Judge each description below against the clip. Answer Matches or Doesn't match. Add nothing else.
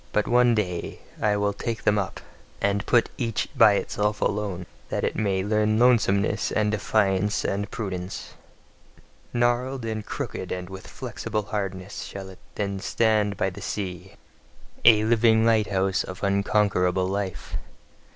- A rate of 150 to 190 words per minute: Doesn't match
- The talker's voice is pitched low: Matches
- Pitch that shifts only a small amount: Matches